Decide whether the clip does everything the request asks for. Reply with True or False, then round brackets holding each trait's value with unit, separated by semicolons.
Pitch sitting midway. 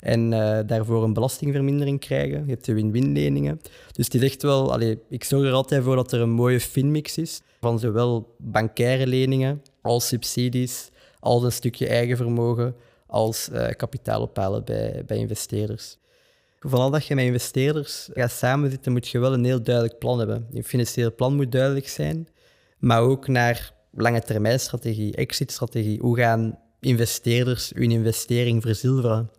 False (120 Hz)